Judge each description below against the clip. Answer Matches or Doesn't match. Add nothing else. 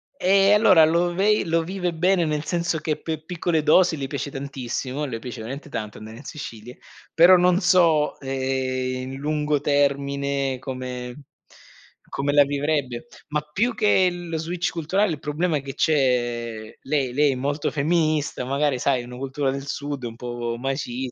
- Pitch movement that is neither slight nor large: Matches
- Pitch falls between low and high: Matches